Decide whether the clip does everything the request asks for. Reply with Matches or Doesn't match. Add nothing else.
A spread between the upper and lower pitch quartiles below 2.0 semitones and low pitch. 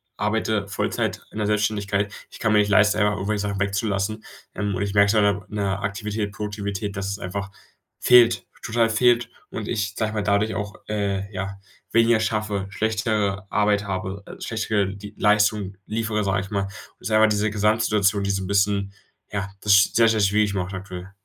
Matches